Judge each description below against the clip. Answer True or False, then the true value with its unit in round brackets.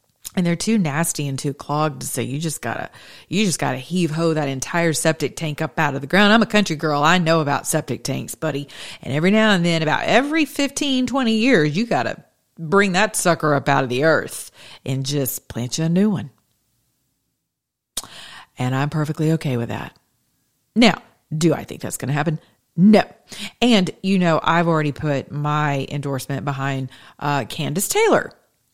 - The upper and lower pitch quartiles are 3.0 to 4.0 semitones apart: False (5.1 semitones)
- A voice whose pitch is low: False (155 Hz)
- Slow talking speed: False (180 wpm)